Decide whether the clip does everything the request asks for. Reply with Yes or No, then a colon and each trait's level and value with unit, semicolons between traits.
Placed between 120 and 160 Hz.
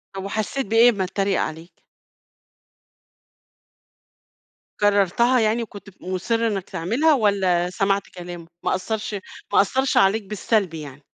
No: high, 200 Hz